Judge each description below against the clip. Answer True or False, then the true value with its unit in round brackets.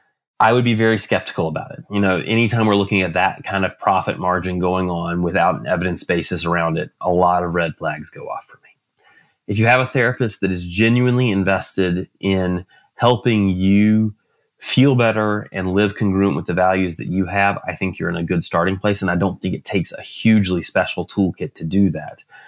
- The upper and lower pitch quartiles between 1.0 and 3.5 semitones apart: True (3.1 semitones)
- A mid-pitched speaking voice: False (95 Hz)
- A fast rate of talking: True (210 wpm)